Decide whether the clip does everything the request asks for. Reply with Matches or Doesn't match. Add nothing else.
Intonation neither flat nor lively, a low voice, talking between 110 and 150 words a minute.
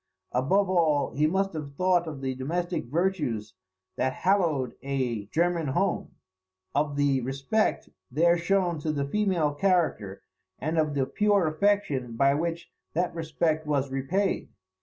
Doesn't match